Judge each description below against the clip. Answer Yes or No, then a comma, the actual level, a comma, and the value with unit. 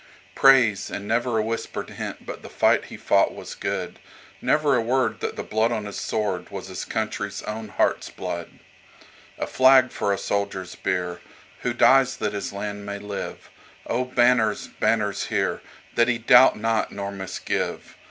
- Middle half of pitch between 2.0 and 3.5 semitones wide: Yes, average, 3.2 semitones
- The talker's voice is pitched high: No, low, 110 Hz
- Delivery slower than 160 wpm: Yes, average, 150 wpm